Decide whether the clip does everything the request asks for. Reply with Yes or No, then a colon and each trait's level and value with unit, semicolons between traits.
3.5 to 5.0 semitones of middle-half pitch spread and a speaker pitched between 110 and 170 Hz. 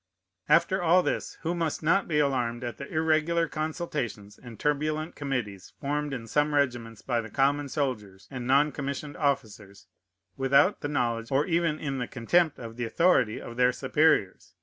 Yes: average, 4.5 semitones; medium, 140 Hz